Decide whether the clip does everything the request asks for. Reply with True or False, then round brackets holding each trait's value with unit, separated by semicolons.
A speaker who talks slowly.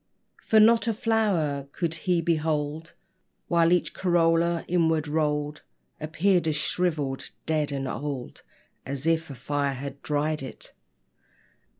True (125 wpm)